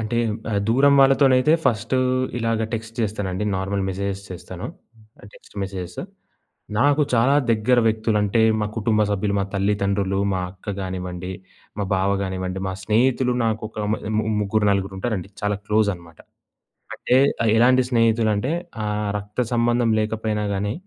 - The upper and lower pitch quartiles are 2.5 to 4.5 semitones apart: Yes, average, 2.8 semitones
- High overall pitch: No, low, 105 Hz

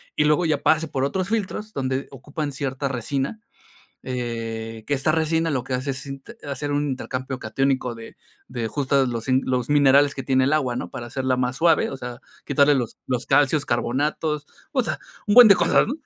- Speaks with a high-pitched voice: No, low, 135 Hz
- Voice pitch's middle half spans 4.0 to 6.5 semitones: No, average, 2.8 semitones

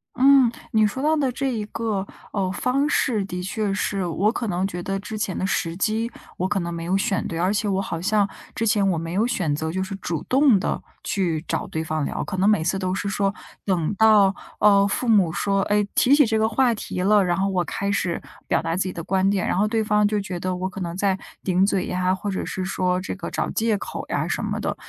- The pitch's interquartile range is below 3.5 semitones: Yes, average, 2.7 semitones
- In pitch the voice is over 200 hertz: No, high, 195 Hz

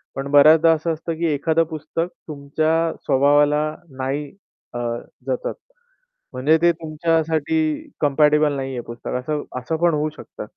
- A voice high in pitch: No, medium, 150 Hz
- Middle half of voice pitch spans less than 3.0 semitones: Yes, narrow, 2.4 semitones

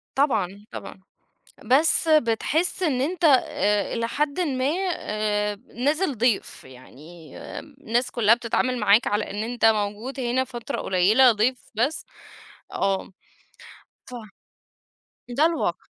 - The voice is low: No, high, 240 Hz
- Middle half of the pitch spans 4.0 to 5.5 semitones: Yes, average, 4.9 semitones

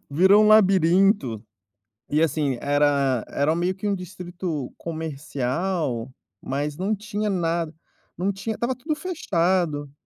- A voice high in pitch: No, medium, 170 Hz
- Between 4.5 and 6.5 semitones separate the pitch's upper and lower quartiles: Yes, average, 5.2 semitones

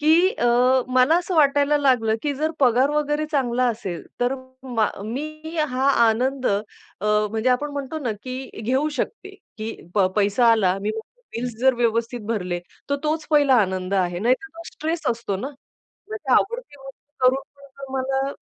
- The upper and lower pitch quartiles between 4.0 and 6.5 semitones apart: Yes, average, 4.5 semitones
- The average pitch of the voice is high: Yes, very high, 260 Hz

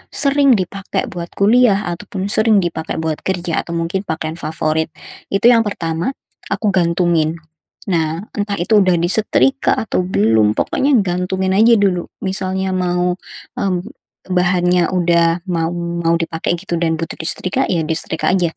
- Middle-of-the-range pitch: Yes, medium, 180 Hz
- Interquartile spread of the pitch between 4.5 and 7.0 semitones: No, average, 2.8 semitones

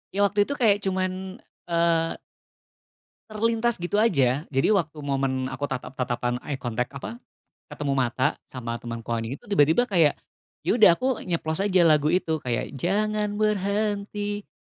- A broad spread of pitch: Yes, wide, 7.3 semitones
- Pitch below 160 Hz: No, medium, 170 Hz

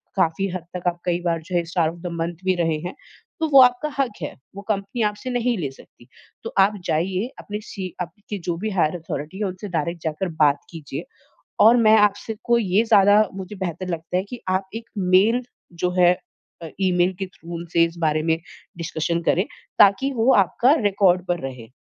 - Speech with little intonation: No, average, 3.6 semitones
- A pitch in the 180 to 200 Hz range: Yes, medium, 185 Hz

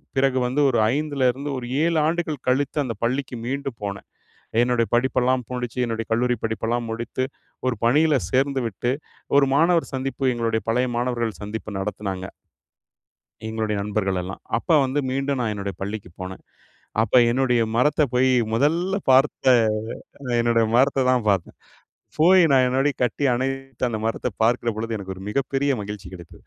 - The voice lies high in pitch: No, low, 125 Hz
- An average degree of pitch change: Yes, average, 3.3 semitones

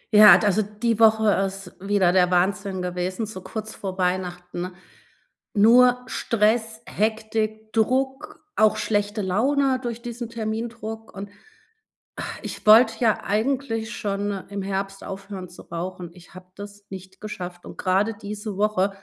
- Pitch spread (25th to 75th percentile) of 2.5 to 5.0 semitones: Yes, average, 2.8 semitones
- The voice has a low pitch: No, high, 205 Hz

